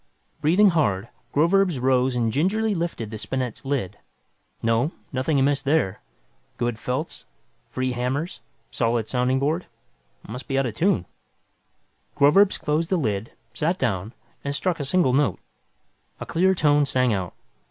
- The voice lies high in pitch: No, low, 135 Hz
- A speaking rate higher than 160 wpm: No, average, 140 wpm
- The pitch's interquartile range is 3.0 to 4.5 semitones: No, average, 5.2 semitones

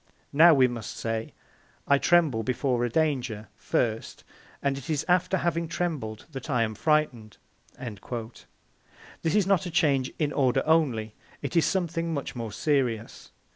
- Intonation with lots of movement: Yes, wide, 5.7 semitones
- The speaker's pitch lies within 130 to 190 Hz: Yes, medium, 140 Hz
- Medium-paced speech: Yes, average, 150 wpm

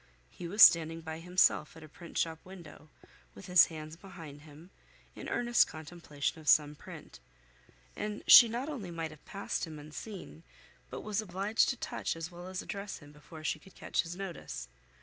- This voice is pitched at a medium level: Yes, medium, 170 Hz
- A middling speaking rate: Yes, average, 180 wpm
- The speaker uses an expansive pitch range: No, average, 3.7 semitones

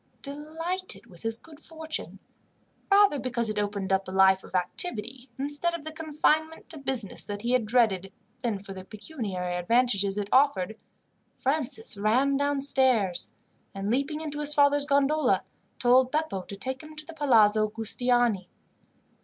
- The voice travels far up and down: Yes, wide, 6.3 semitones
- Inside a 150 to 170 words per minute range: Yes, average, 155 wpm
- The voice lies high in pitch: Yes, very high, 255 Hz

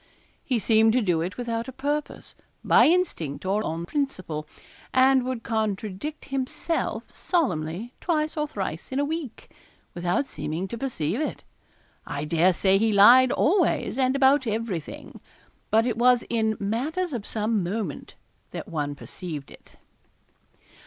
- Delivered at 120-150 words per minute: Yes, average, 145 wpm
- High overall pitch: Yes, high, 225 Hz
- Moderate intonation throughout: No, wide, 6.3 semitones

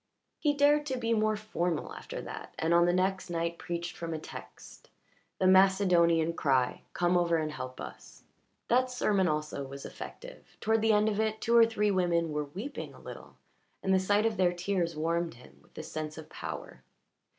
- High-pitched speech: No, medium, 180 Hz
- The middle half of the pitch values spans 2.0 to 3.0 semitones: No, average, 4.5 semitones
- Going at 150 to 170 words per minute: No, average, 195 wpm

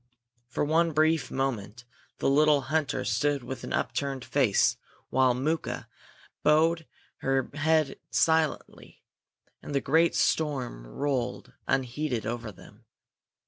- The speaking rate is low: Yes, slow, 110 wpm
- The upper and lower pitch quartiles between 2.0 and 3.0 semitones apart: No, average, 3.5 semitones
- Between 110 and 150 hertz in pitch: Yes, medium, 140 Hz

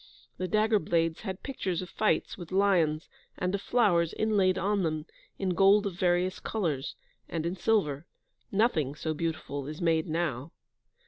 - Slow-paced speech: No, average, 155 wpm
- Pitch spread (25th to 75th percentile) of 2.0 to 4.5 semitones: Yes, average, 3.7 semitones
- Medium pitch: Yes, medium, 175 Hz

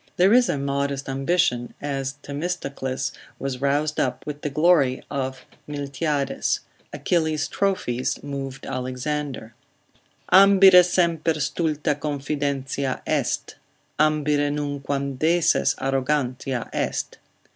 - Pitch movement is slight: Yes, narrow, 2.3 semitones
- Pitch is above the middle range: No, medium, 145 Hz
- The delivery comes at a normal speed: No, slow, 100 wpm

